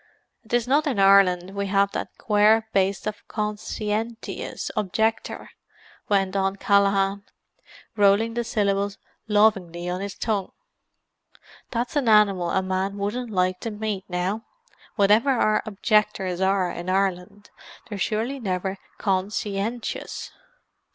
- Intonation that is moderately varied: No, narrow, 2.2 semitones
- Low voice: No, high, 200 Hz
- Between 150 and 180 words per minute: No, average, 140 wpm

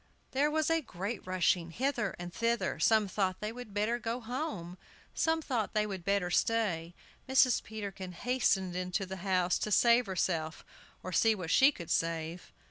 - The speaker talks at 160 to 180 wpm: Yes, average, 165 wpm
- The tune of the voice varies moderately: Yes, average, 4.7 semitones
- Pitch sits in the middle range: No, high, 200 Hz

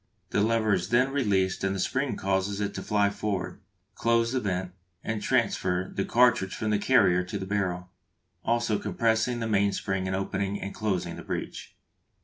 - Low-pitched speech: Yes, low, 100 Hz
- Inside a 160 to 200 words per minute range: Yes, average, 175 wpm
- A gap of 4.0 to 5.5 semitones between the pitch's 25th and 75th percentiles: No, average, 3.0 semitones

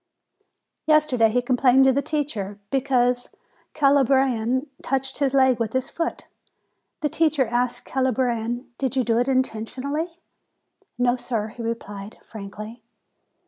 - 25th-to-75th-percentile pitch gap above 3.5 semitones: No, average, 2.7 semitones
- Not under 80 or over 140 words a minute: Yes, slow, 135 wpm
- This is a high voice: Yes, very high, 255 Hz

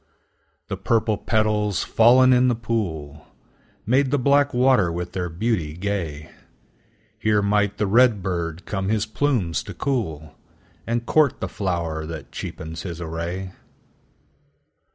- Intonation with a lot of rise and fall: Yes, wide, 5.7 semitones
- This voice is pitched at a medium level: No, low, 100 Hz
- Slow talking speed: Yes, slow, 120 wpm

